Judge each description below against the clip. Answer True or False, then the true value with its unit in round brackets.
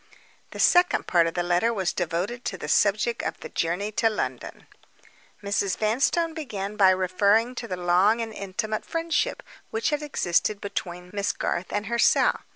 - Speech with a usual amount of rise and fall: True (4.2 semitones)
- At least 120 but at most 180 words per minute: True (165 wpm)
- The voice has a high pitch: True (205 Hz)